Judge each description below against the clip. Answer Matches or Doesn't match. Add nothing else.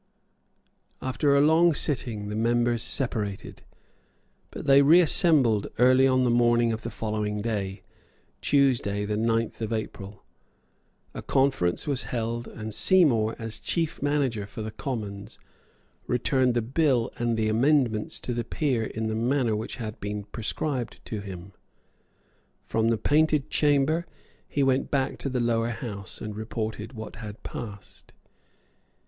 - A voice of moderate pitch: Doesn't match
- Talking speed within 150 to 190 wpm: Doesn't match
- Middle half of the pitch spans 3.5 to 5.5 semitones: Matches